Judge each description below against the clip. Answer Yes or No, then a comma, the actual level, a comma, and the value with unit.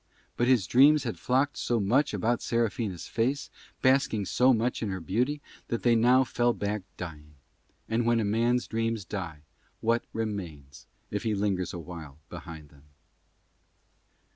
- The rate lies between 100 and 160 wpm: Yes, average, 150 wpm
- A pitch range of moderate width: Yes, average, 4.8 semitones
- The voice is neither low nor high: No, low, 115 Hz